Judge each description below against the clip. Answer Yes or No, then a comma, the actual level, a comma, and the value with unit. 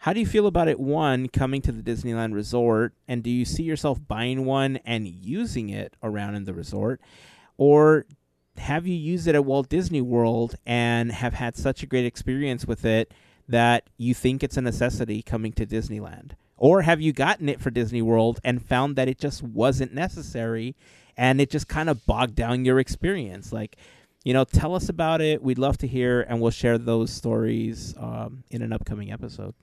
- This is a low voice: Yes, low, 120 Hz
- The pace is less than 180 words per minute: No, average, 200 wpm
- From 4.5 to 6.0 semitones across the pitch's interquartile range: No, average, 3.2 semitones